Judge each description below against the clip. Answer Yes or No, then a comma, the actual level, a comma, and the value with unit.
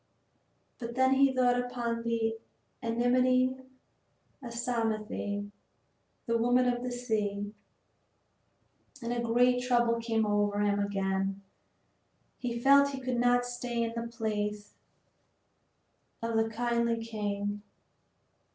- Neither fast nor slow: No, slow, 110 wpm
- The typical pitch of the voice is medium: No, high, 235 Hz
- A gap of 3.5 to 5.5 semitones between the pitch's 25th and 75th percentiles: No, narrow, 2.5 semitones